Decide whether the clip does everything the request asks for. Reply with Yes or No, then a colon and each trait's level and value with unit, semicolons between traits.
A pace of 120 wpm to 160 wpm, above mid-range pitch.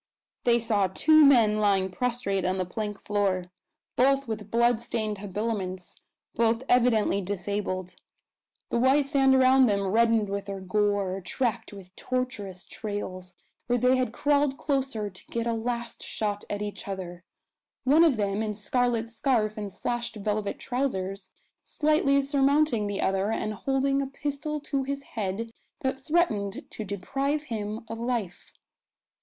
Yes: average, 145 wpm; high, 225 Hz